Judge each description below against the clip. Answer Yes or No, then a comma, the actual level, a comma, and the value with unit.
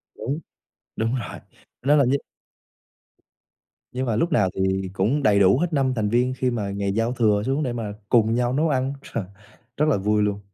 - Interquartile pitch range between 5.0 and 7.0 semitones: No, average, 4.3 semitones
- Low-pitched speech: Yes, low, 120 Hz